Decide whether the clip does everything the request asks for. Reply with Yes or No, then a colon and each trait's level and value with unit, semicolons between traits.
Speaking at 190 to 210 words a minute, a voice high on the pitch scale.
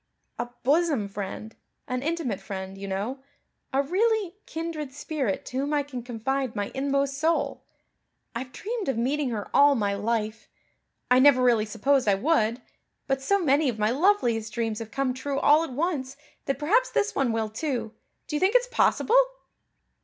No: average, 175 wpm; very high, 265 Hz